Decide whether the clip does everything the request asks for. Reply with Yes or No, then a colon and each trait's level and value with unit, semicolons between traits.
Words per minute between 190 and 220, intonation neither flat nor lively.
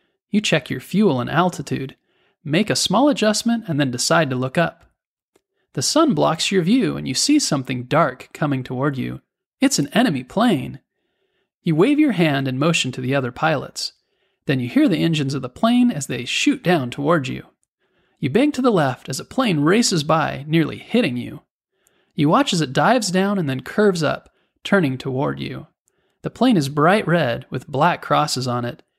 No: average, 195 wpm; wide, 7.9 semitones